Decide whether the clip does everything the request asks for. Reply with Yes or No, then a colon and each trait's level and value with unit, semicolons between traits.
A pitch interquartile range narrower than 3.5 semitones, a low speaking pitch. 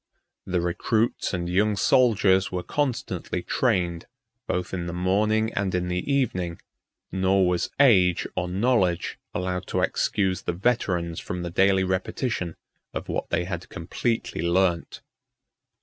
Yes: average, 2.8 semitones; very low, 95 Hz